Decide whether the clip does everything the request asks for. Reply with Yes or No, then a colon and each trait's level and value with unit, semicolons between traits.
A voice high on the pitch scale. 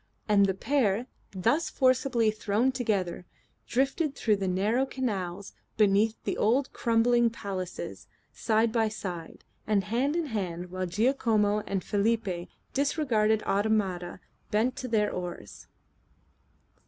Yes: high, 215 Hz